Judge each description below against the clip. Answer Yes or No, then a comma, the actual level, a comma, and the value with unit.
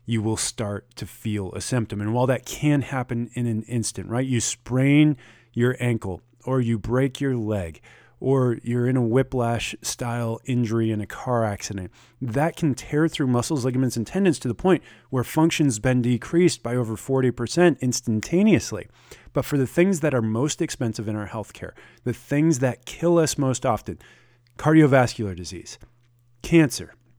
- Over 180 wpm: No, average, 170 wpm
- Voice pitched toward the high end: No, low, 120 Hz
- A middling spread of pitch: Yes, average, 3.0 semitones